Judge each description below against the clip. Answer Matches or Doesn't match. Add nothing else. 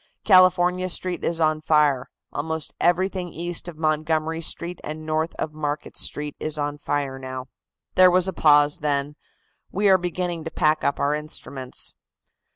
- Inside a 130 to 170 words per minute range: Matches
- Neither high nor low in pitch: Matches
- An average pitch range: Matches